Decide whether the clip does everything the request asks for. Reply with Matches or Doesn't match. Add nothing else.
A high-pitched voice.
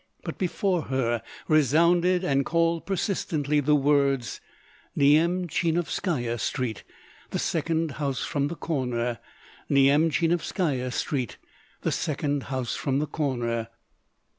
Doesn't match